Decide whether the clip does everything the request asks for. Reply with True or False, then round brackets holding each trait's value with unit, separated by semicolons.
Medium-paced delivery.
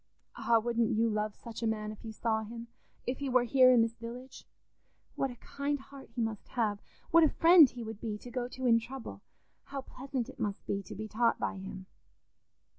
False (210 wpm)